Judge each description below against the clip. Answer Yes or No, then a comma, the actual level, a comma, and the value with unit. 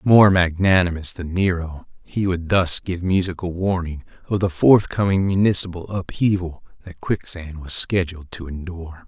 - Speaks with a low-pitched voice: Yes, very low, 90 Hz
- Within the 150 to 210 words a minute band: No, average, 140 wpm